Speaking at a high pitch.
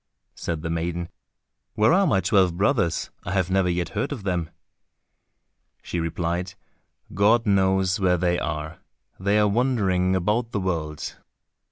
No: very low, 95 Hz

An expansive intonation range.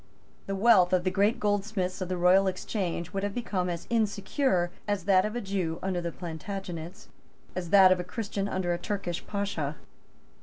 No: narrow, 2.4 semitones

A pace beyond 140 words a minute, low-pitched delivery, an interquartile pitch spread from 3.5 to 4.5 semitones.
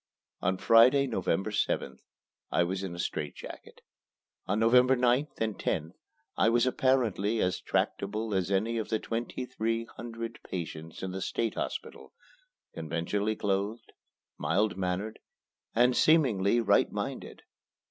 No: slow, 135 wpm; low, 110 Hz; average, 3.8 semitones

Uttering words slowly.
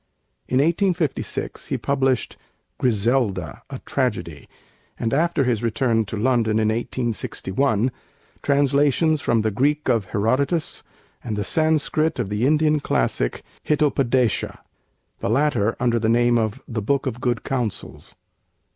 Yes: slow, 130 wpm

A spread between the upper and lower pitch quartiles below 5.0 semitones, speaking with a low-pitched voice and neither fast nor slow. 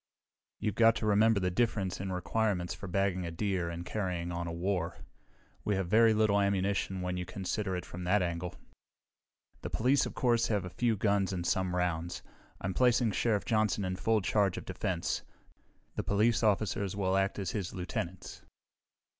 Yes: average, 3.0 semitones; very low, 95 Hz; average, 180 wpm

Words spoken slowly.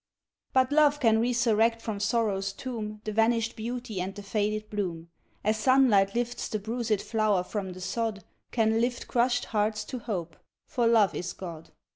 No: average, 165 wpm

